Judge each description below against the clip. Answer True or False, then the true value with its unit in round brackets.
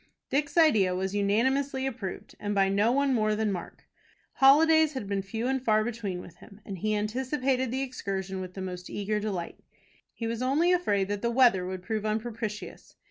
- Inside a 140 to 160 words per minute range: False (190 wpm)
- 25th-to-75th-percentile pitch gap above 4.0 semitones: True (4.9 semitones)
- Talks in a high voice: True (215 Hz)